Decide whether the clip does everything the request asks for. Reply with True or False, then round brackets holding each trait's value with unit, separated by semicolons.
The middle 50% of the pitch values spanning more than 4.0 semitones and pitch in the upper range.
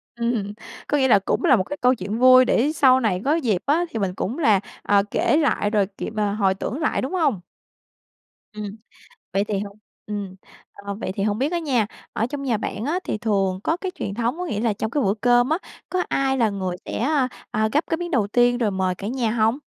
True (4.9 semitones; 230 Hz)